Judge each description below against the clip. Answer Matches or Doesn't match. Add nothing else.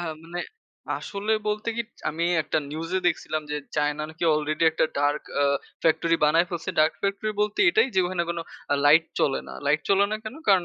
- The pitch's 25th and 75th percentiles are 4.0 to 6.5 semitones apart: Matches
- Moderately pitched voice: Matches